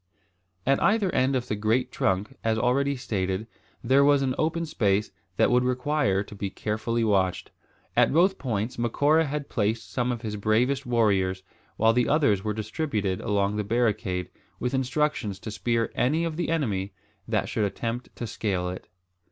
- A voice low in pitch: Yes, low, 115 Hz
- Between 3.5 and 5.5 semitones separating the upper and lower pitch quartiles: Yes, average, 4.8 semitones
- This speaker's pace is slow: No, average, 170 wpm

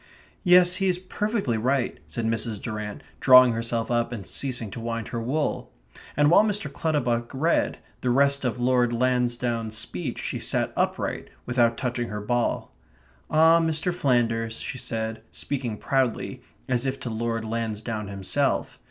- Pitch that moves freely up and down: No, average, 3.5 semitones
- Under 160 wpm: Yes, average, 150 wpm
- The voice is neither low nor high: No, low, 120 Hz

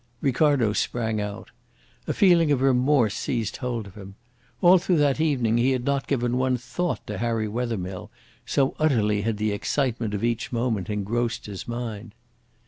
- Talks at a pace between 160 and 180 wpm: Yes, average, 165 wpm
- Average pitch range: Yes, average, 4.0 semitones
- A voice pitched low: Yes, low, 120 Hz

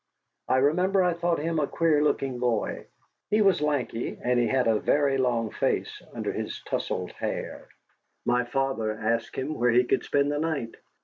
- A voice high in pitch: No, low, 135 Hz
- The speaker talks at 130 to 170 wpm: No, average, 180 wpm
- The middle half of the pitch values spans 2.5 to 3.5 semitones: No, average, 4.3 semitones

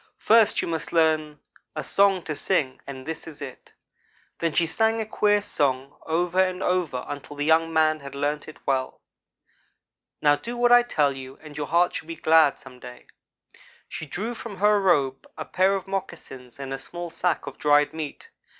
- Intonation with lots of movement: No, average, 4.4 semitones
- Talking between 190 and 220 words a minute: Yes, average, 195 wpm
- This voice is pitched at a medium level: Yes, medium, 160 Hz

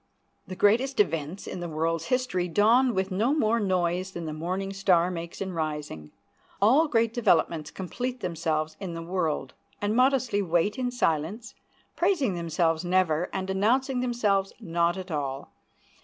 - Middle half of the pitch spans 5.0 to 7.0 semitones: Yes, average, 5.3 semitones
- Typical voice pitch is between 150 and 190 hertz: Yes, medium, 185 Hz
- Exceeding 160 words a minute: No, average, 155 wpm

